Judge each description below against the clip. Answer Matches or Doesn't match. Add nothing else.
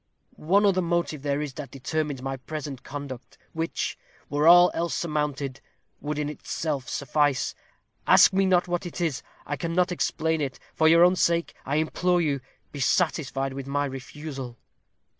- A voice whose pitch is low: Doesn't match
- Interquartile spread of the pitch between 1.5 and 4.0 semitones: Matches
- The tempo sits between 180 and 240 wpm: Doesn't match